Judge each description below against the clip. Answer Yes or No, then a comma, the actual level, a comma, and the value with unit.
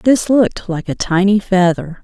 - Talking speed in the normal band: Yes, average, 175 wpm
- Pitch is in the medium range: No, high, 195 Hz